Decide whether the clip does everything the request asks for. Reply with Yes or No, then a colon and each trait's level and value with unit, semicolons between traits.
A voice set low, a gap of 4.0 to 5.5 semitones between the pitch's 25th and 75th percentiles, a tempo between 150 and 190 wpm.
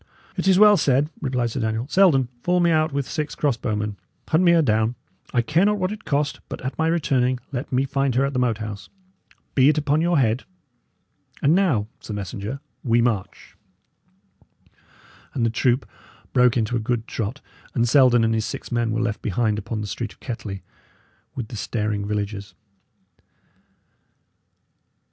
Yes: low, 125 Hz; average, 4.8 semitones; average, 175 wpm